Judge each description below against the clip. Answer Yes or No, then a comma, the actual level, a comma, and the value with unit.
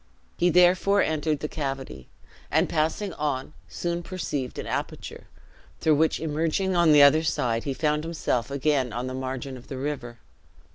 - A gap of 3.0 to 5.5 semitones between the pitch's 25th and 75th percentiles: Yes, average, 3.6 semitones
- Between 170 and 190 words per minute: No, average, 160 wpm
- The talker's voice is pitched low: No, medium, 150 Hz